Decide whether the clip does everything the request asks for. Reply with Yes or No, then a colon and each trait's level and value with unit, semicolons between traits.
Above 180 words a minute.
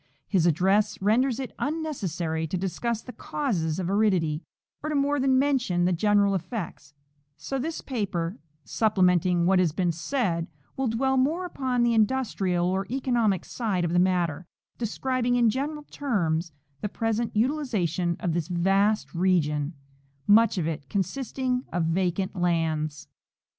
No: average, 145 wpm